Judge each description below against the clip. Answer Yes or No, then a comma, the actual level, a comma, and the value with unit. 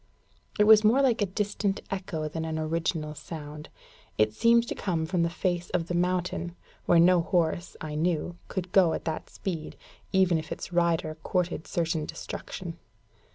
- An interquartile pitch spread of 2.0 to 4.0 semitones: Yes, narrow, 2.6 semitones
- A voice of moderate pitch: Yes, medium, 175 Hz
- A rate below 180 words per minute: Yes, average, 170 wpm